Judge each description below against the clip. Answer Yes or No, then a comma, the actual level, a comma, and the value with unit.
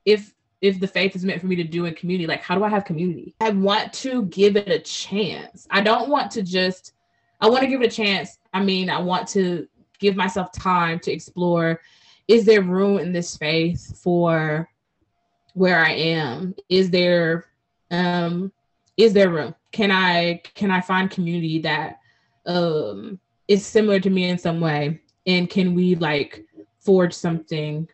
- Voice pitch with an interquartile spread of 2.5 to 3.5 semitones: Yes, average, 3.0 semitones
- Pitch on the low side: No, medium, 180 Hz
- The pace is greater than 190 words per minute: No, average, 180 wpm